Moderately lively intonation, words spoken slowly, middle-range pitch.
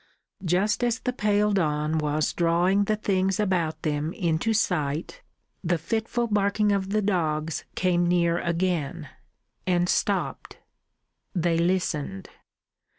Yes: average, 3.9 semitones; slow, 115 wpm; medium, 180 Hz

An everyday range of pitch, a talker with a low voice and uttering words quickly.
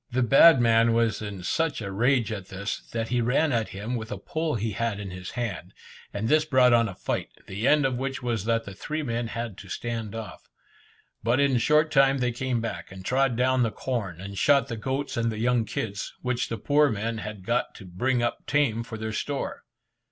Yes: average, 3.3 semitones; low, 115 Hz; fast, 225 wpm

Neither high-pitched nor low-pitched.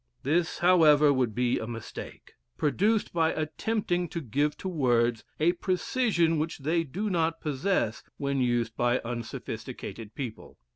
Yes: medium, 150 Hz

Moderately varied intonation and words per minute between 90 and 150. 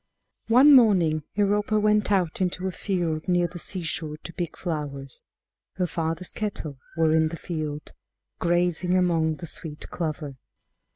Yes: average, 3.1 semitones; average, 140 wpm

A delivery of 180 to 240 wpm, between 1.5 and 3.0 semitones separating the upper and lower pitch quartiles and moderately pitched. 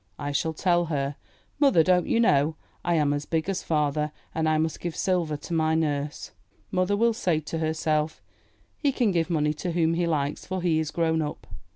Yes: fast, 205 wpm; narrow, 2.6 semitones; medium, 160 Hz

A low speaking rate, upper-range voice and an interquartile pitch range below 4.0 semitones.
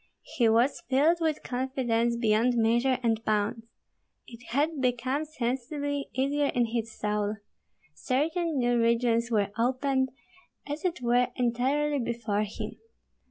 Yes: slow, 125 wpm; high, 245 Hz; average, 3.3 semitones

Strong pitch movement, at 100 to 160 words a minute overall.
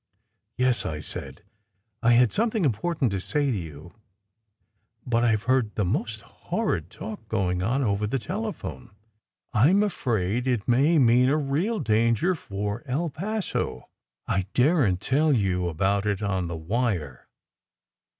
Yes: wide, 5.8 semitones; average, 155 wpm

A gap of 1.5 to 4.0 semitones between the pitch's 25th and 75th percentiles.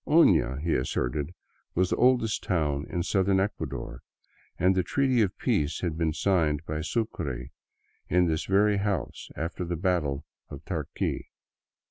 No: average, 4.5 semitones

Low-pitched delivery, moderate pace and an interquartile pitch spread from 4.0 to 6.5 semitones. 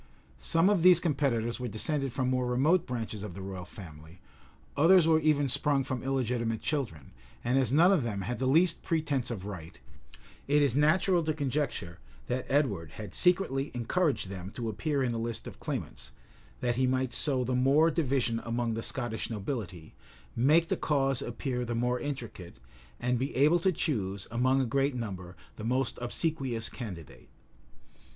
Yes: low, 125 Hz; average, 175 wpm; average, 4.5 semitones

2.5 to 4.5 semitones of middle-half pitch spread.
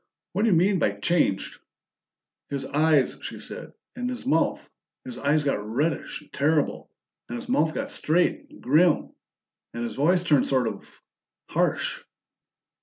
No: average, 4.9 semitones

